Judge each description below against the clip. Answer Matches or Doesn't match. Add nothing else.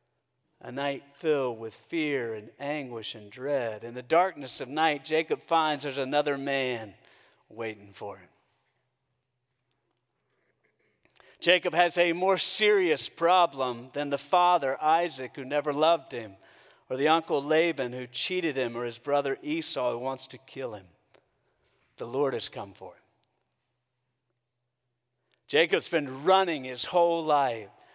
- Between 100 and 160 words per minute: Matches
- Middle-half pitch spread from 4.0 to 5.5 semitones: Matches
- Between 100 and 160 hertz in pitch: Matches